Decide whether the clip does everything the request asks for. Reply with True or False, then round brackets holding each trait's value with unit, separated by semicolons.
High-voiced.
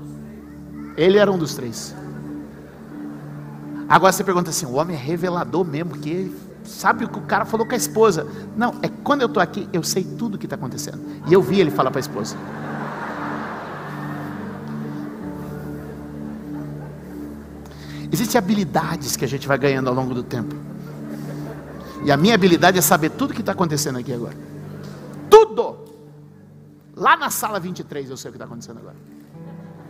False (125 Hz)